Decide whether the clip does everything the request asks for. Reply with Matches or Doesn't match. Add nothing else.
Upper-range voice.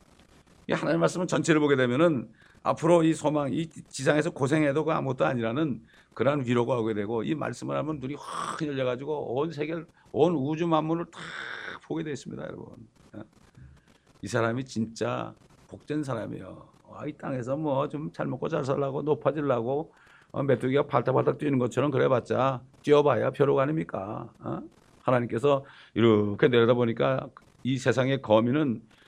Doesn't match